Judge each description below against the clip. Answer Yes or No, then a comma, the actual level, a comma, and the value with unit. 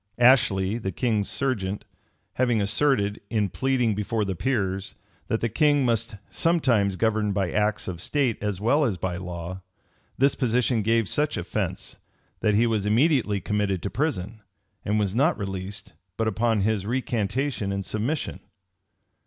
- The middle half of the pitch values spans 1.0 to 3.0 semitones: No, average, 3.9 semitones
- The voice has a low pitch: Yes, low, 110 Hz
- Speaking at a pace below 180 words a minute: Yes, average, 150 wpm